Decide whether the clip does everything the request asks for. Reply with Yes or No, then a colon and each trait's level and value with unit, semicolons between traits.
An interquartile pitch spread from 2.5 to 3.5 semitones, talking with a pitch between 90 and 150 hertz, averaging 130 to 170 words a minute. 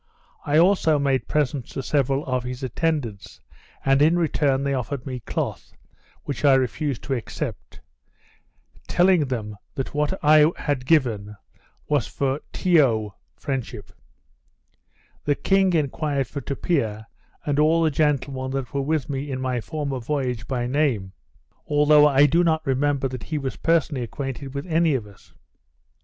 Yes: average, 2.9 semitones; medium, 140 Hz; average, 150 wpm